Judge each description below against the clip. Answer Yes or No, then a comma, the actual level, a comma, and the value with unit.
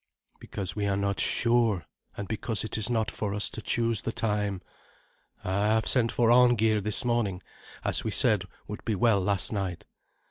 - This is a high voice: No, low, 105 Hz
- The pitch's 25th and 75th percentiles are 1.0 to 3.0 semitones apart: Yes, narrow, 2.5 semitones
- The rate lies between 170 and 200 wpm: Yes, average, 180 wpm